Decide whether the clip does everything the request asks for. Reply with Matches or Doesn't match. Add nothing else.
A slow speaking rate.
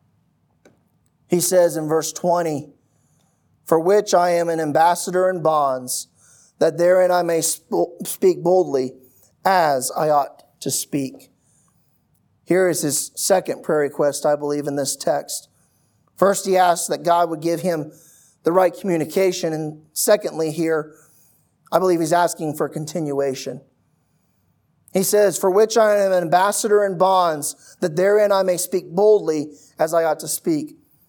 Doesn't match